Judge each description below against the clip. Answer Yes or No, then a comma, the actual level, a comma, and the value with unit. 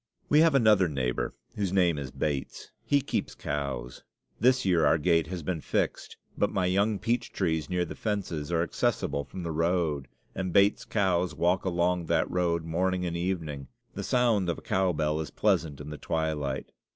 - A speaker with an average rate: Yes, average, 185 wpm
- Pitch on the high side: No, very low, 85 Hz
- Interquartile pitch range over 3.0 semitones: Yes, average, 3.6 semitones